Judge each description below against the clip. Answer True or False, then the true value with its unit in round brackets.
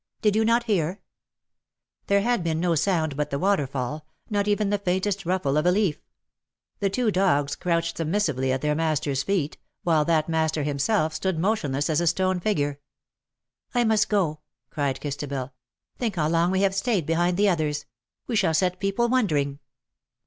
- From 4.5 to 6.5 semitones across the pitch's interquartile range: True (5.0 semitones)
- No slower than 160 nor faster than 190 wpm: True (185 wpm)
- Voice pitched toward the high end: False (170 Hz)